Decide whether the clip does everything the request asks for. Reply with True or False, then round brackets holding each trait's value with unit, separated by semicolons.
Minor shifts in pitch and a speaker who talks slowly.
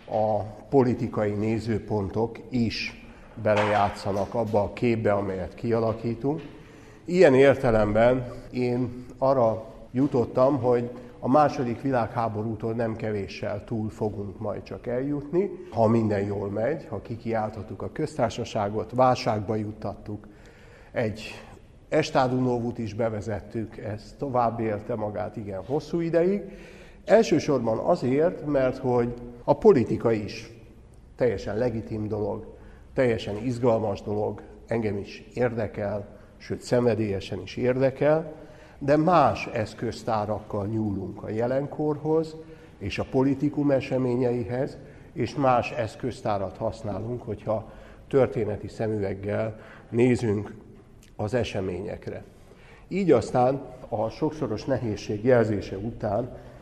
False (3.3 semitones; 100 wpm)